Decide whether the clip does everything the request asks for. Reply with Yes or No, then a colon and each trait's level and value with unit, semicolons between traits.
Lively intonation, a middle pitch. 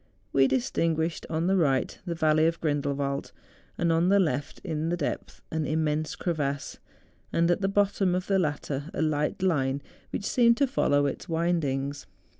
No: average, 3.6 semitones; medium, 160 Hz